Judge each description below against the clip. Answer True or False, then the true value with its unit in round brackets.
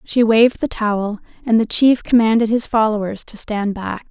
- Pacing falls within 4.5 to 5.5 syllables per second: True (5.1 syllables/s)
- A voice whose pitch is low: False (220 Hz)